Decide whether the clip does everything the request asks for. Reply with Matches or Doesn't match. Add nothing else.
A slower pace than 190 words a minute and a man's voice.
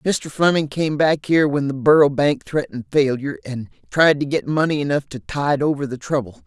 Doesn't match